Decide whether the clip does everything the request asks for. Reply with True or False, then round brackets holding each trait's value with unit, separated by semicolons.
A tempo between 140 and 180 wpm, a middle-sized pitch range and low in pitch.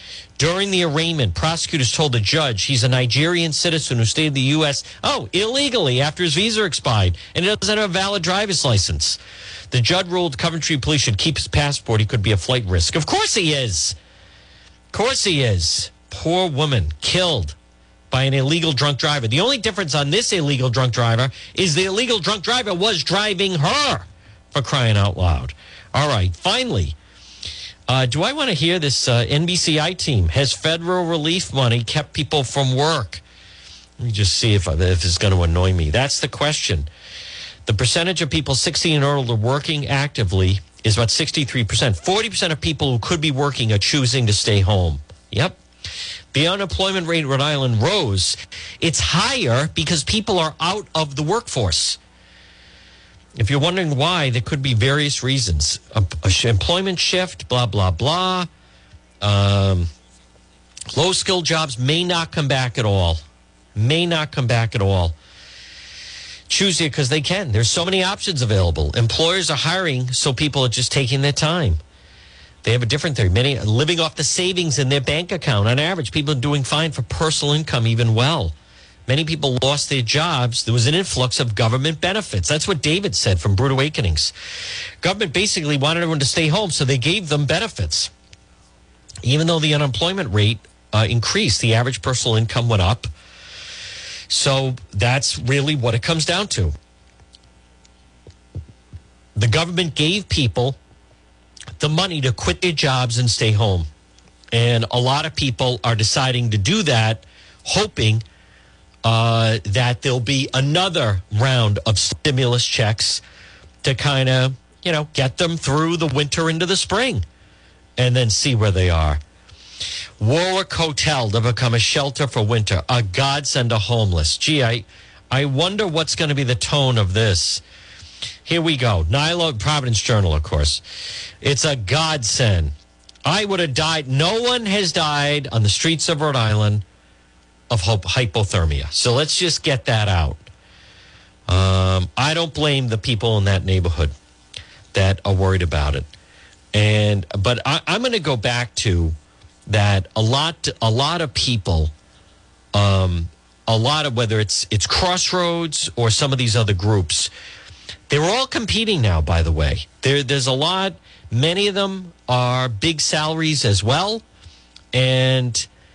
False (165 wpm; 7.7 semitones; 125 Hz)